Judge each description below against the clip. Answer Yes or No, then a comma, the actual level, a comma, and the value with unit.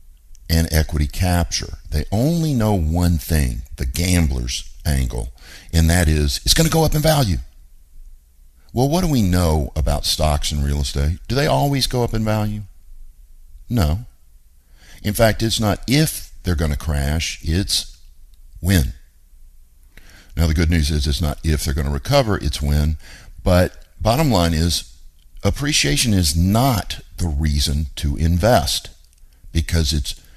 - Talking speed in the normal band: Yes, average, 150 wpm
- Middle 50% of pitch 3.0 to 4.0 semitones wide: No, average, 4.9 semitones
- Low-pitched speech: Yes, very low, 80 Hz